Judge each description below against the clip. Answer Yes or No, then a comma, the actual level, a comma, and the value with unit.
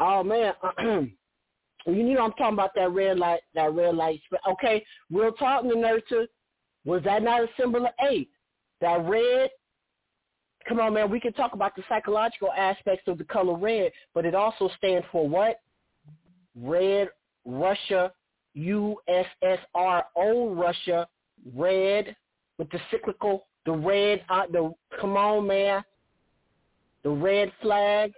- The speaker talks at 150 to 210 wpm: No, average, 140 wpm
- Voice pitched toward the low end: No, high, 195 Hz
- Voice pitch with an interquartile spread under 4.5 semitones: Yes, average, 3.7 semitones